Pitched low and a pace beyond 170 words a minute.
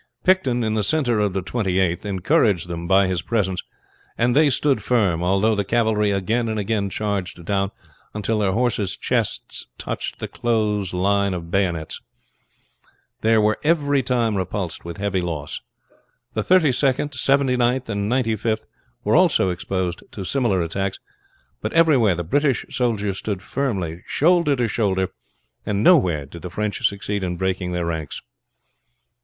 No: low, 105 Hz; average, 160 wpm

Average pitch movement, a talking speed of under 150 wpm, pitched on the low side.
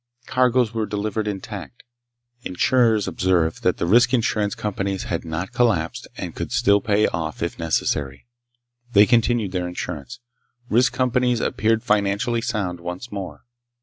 Yes: average, 4.7 semitones; average, 140 wpm; low, 105 Hz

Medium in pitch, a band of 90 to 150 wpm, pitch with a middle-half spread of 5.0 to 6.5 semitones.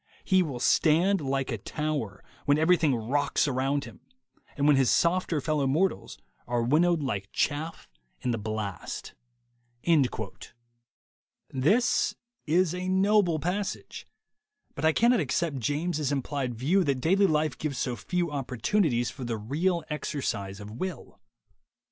Yes: medium, 150 Hz; average, 140 wpm; average, 5.3 semitones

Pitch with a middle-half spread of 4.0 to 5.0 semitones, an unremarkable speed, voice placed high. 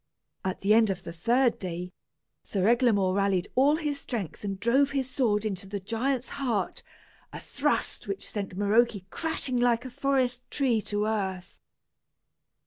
Yes: average, 4.7 semitones; average, 155 wpm; high, 220 Hz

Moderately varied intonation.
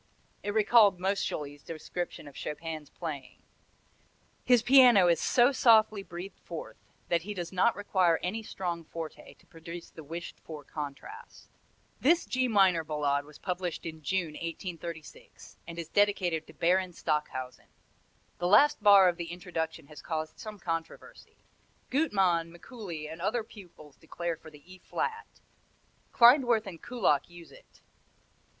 Yes: average, 4.2 semitones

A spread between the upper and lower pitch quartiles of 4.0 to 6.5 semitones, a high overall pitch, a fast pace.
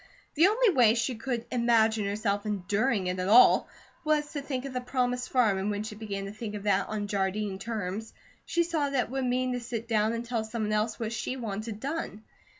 No: average, 3.3 semitones; high, 225 Hz; fast, 220 wpm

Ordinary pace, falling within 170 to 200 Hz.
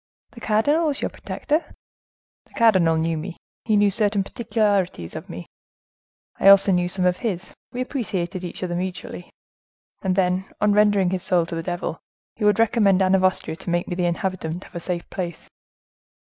Yes: average, 185 wpm; medium, 185 Hz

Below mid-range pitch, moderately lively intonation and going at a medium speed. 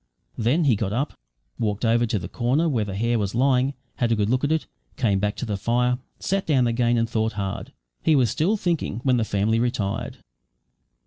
No: low, 120 Hz; average, 3.5 semitones; fast, 210 wpm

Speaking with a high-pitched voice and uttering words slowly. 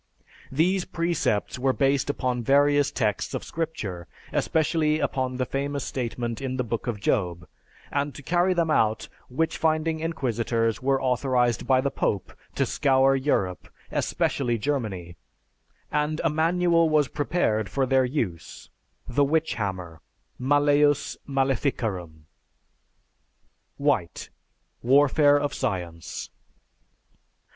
No: low, 135 Hz; slow, 120 wpm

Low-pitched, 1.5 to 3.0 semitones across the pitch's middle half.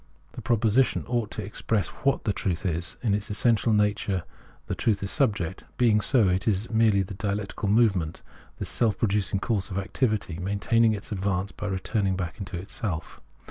Yes: low, 100 Hz; average, 2.7 semitones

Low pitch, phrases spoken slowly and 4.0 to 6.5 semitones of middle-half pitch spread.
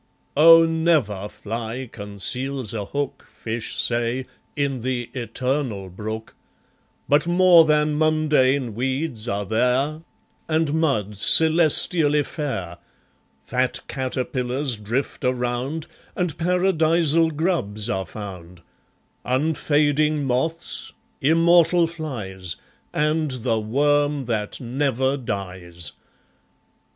Yes: low, 130 Hz; slow, 95 wpm; wide, 5.6 semitones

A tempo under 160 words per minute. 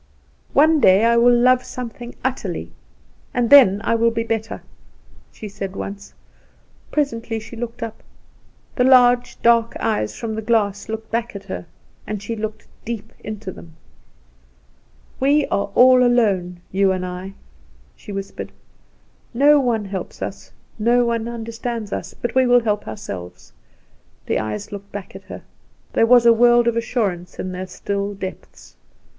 Yes: average, 150 wpm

